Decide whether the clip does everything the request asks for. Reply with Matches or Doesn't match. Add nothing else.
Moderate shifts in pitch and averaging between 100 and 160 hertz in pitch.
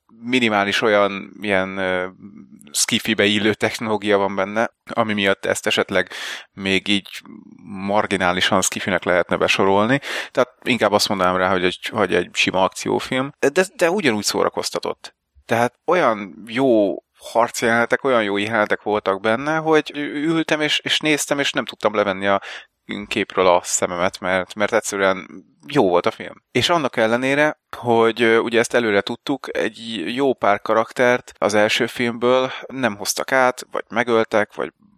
Matches